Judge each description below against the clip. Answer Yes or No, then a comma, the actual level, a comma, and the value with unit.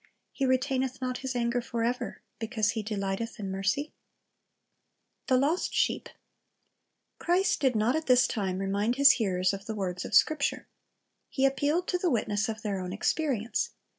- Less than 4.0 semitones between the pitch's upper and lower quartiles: No, average, 4.7 semitones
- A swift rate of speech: No, average, 165 wpm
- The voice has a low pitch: No, high, 235 Hz